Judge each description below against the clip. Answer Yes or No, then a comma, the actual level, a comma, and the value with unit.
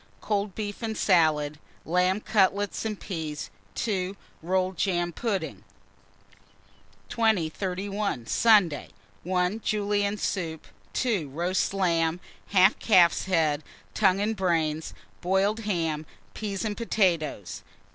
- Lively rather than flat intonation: No, average, 3.8 semitones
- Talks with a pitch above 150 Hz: Yes, medium, 185 Hz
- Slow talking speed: Yes, slow, 105 wpm